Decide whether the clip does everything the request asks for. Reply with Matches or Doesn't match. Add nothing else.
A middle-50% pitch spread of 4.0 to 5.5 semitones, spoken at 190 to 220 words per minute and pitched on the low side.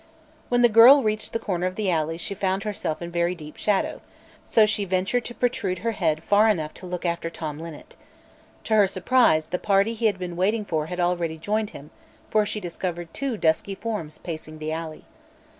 Doesn't match